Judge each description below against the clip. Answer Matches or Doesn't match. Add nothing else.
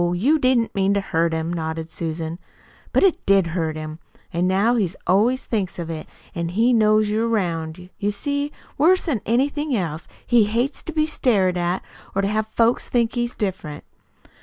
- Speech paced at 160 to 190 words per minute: Matches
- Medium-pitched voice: Doesn't match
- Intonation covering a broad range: Matches